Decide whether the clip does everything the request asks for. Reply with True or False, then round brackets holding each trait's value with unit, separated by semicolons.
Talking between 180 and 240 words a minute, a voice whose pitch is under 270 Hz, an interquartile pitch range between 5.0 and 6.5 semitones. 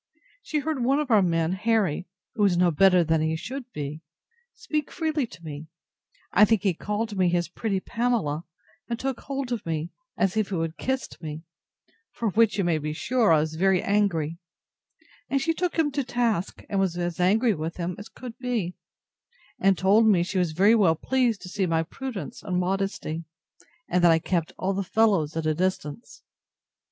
True (195 wpm; 190 Hz; 5.5 semitones)